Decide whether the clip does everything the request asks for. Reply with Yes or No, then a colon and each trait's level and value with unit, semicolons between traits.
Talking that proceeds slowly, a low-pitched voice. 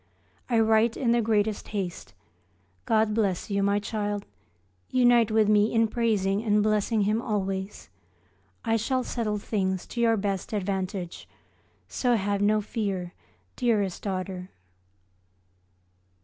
No: slow, 125 wpm; high, 210 Hz